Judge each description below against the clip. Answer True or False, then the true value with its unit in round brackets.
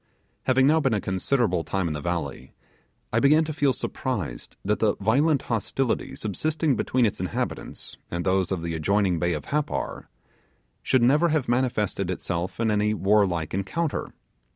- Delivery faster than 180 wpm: False (160 wpm)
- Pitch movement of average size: False (6.6 semitones)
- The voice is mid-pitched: False (105 Hz)